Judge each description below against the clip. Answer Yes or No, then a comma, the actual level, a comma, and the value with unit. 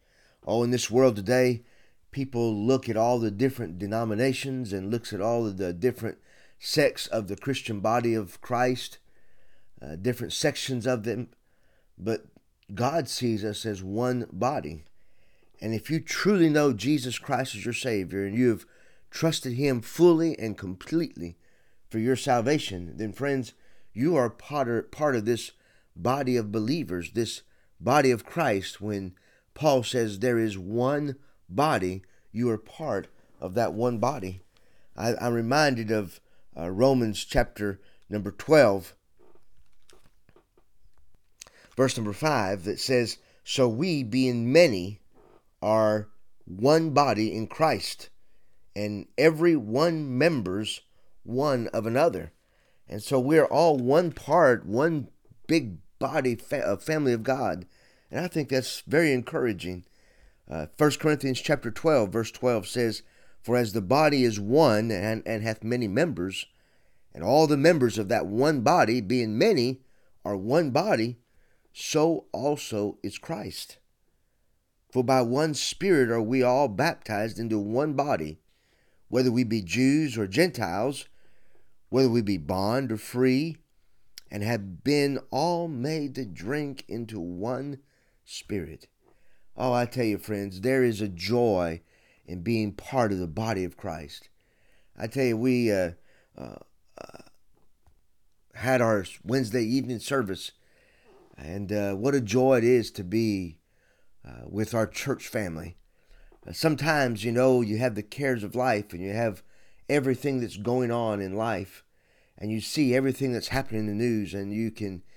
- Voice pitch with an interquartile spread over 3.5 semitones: Yes, average, 4.2 semitones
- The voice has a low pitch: Yes, low, 120 Hz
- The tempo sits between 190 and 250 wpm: No, average, 145 wpm